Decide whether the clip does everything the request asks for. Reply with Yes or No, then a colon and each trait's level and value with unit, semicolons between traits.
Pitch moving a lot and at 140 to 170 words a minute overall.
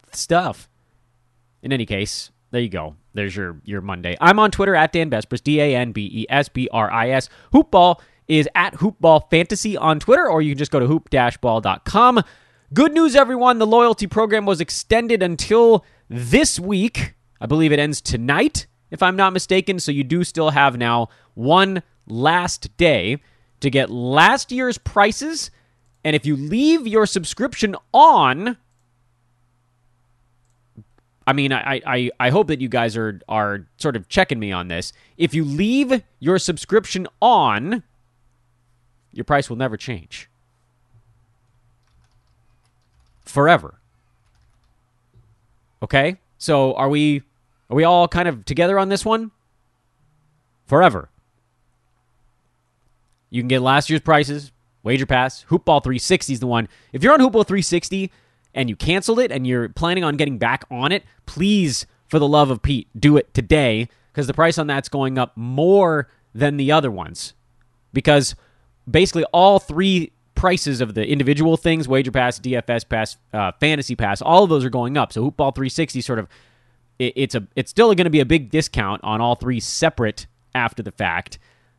Yes: wide, 5.7 semitones; average, 165 wpm